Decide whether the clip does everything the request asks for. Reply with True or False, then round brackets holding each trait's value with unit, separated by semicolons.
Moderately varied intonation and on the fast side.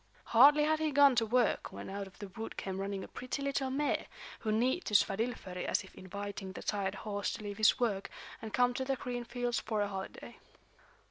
True (4.1 semitones; 215 wpm)